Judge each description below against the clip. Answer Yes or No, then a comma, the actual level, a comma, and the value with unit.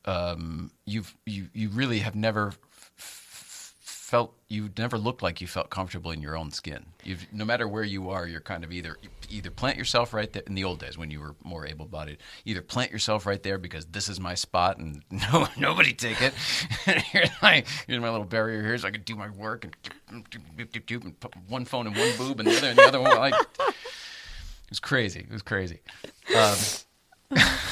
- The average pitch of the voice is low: Yes, low, 105 Hz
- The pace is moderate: No, fast, 215 wpm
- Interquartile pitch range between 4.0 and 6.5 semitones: Yes, average, 4.6 semitones